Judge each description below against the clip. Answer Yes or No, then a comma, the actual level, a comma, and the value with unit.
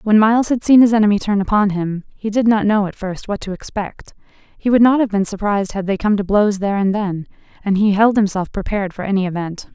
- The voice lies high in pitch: Yes, high, 205 Hz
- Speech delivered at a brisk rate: Yes, fast, 245 wpm